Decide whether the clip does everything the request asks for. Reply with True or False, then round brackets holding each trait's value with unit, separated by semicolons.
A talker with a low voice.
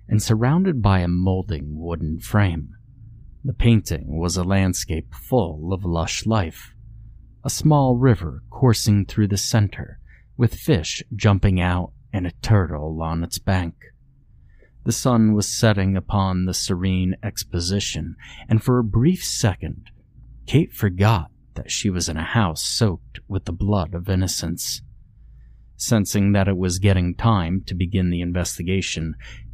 True (100 Hz)